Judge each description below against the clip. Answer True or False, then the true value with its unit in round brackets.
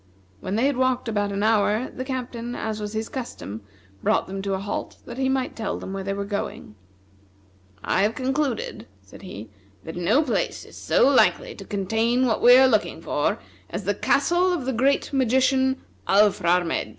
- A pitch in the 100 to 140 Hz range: False (230 Hz)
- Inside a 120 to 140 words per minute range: False (185 wpm)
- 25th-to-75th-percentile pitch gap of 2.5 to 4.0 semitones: False (4.6 semitones)